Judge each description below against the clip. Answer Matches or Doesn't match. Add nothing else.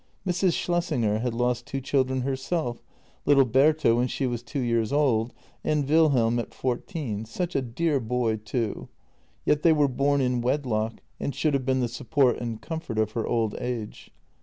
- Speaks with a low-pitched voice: Matches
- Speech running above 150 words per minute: Matches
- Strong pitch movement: Doesn't match